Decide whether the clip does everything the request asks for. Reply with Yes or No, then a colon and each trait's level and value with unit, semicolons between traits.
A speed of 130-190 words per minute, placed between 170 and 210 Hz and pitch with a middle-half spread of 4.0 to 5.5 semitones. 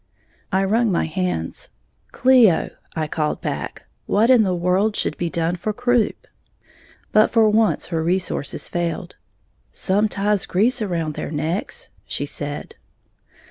Yes: average, 140 wpm; high, 190 Hz; average, 4.4 semitones